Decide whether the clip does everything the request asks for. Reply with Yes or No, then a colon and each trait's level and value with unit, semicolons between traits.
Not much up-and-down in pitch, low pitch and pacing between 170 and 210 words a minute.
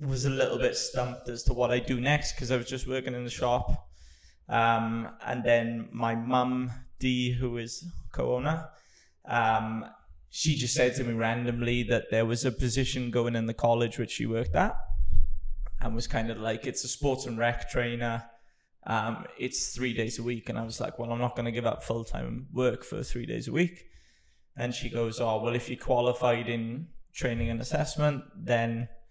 Yes: narrow, 1.7 semitones; low, 120 Hz; average, 200 wpm